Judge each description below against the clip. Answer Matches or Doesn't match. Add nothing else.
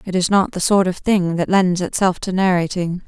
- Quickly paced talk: Matches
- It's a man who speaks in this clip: Doesn't match